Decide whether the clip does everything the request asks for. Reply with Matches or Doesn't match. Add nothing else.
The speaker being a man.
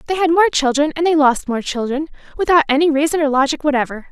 Doesn't match